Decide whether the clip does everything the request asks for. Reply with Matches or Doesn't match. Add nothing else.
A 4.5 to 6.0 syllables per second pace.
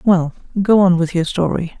Matches